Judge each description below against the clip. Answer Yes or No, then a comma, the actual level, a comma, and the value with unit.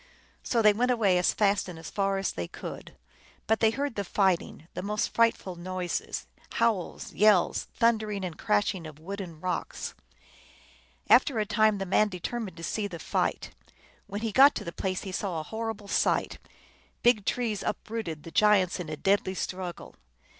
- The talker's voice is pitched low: No, high, 200 Hz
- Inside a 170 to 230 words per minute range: Yes, average, 175 wpm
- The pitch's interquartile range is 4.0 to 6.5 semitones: No, average, 3.3 semitones